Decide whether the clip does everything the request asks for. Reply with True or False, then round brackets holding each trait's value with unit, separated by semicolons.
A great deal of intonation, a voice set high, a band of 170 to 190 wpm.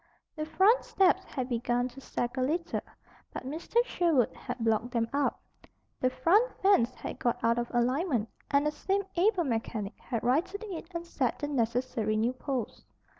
True (6.0 semitones; 260 Hz; 175 wpm)